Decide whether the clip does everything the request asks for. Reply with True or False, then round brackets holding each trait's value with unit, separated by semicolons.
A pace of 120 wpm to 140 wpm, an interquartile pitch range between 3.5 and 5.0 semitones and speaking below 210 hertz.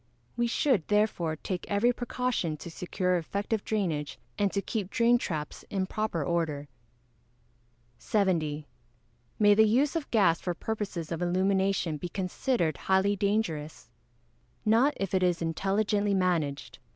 True (135 wpm; 4.3 semitones; 190 Hz)